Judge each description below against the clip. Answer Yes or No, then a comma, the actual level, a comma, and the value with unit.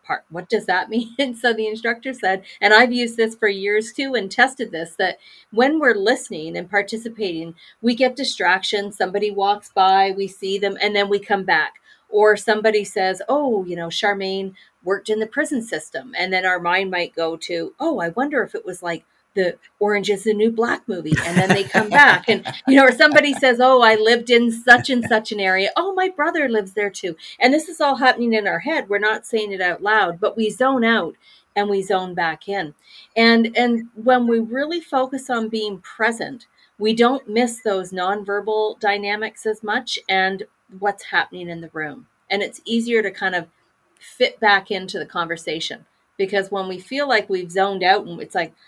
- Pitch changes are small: No, average, 3.8 semitones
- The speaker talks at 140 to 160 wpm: No, fast, 205 wpm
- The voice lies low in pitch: No, high, 215 Hz